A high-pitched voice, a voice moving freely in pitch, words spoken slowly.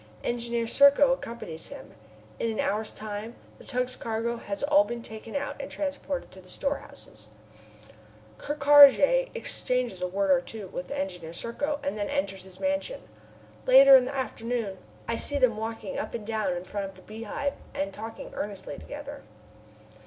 No: high, 230 Hz; wide, 5.7 semitones; average, 165 wpm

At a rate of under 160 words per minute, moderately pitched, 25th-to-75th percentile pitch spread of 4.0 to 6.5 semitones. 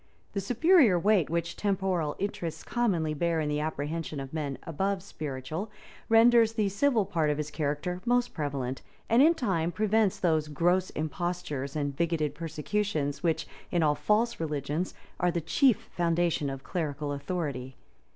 Yes: average, 150 wpm; medium, 170 Hz; average, 5.1 semitones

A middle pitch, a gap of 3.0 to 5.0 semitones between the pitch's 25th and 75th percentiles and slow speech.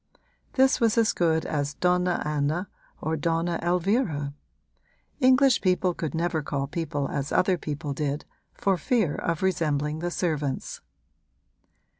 Yes: medium, 165 Hz; average, 3.6 semitones; slow, 130 wpm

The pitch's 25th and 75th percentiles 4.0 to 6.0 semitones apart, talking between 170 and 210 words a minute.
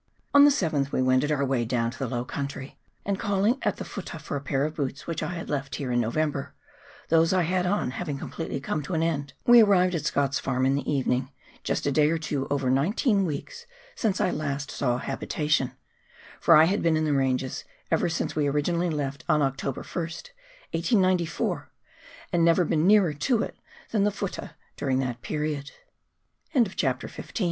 Yes: average, 4.4 semitones; average, 195 wpm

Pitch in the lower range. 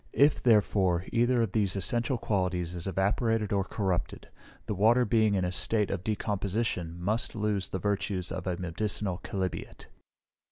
Yes: low, 100 Hz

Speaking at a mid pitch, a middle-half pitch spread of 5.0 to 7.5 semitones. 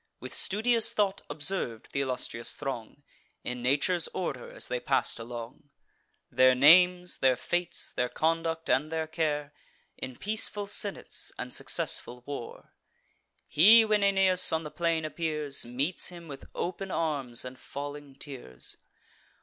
Yes: medium, 150 Hz; wide, 5.5 semitones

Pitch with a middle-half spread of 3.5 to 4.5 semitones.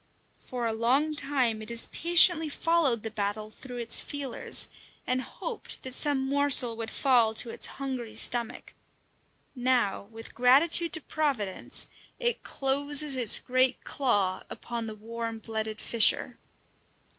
Yes: average, 4.0 semitones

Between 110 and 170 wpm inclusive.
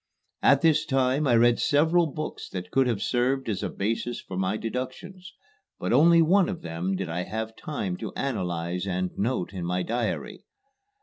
No: average, 180 wpm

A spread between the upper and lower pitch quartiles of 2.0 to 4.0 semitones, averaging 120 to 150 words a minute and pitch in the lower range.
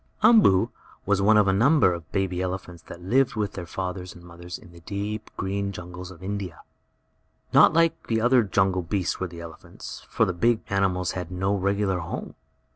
No: narrow, 2.5 semitones; average, 195 wpm; very low, 95 Hz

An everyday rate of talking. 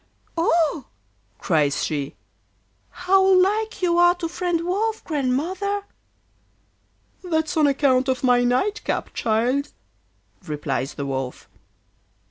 No: slow, 105 wpm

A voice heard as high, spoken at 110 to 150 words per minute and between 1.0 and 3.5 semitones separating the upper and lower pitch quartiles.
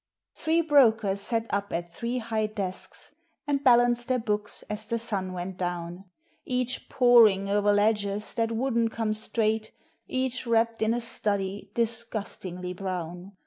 Yes: high, 220 Hz; average, 145 wpm; average, 3.0 semitones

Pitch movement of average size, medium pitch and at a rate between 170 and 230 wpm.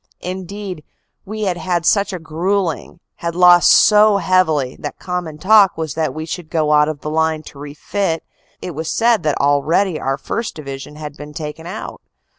Yes: average, 3.7 semitones; medium, 165 Hz; average, 180 wpm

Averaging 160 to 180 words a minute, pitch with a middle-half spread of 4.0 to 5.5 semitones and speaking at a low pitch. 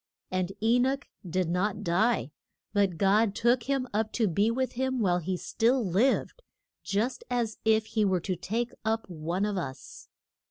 No: average, 170 wpm; average, 4.3 semitones; high, 215 Hz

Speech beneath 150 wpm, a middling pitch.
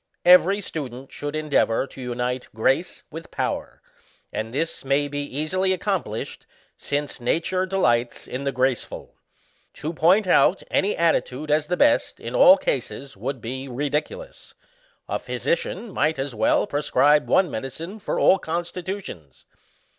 Yes: average, 140 wpm; medium, 150 Hz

